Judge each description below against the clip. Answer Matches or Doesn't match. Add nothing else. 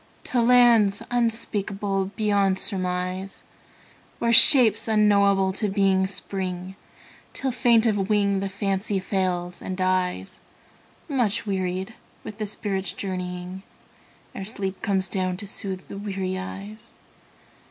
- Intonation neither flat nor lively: Doesn't match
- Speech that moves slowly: Matches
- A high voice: Matches